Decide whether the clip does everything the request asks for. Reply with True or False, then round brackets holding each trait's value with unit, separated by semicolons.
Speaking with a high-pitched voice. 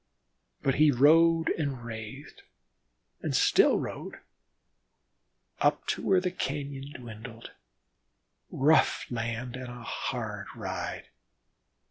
False (130 Hz)